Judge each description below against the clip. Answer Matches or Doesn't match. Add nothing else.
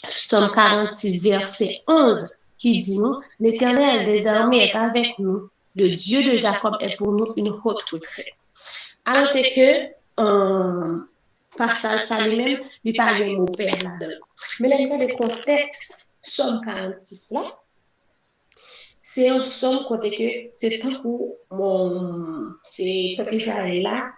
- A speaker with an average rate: Doesn't match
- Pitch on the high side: Matches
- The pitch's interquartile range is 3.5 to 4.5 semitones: Matches